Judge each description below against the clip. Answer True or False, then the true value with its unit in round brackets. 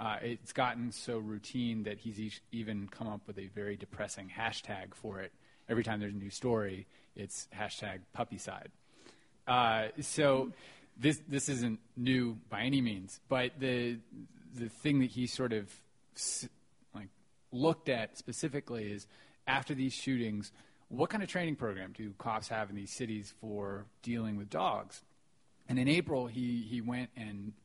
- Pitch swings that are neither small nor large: True (3.5 semitones)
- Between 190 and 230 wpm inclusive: False (170 wpm)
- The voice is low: True (115 Hz)